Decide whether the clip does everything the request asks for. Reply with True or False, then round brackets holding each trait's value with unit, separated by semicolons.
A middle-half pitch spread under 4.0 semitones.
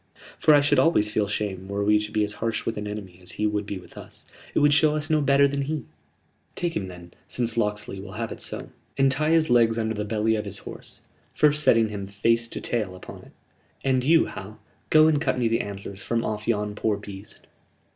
False (4.9 semitones)